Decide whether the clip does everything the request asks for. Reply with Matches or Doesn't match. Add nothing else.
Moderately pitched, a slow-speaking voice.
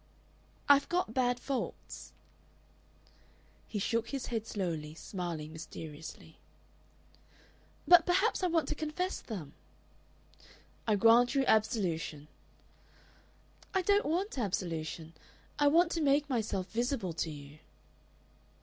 Doesn't match